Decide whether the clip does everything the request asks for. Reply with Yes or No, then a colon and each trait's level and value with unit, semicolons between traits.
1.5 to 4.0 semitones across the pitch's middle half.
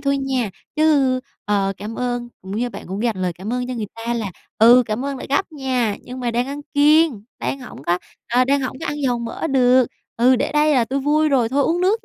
Yes: average, 3.3 semitones